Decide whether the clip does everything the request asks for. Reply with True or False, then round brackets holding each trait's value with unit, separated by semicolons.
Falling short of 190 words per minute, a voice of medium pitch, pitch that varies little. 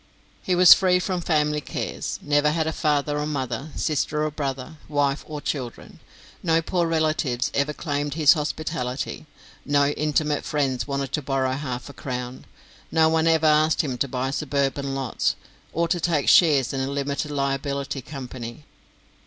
True (160 wpm; 145 Hz; 2.3 semitones)